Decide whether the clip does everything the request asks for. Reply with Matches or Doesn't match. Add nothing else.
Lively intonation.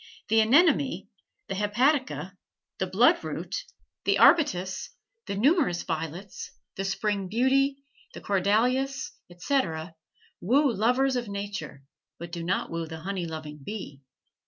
Matches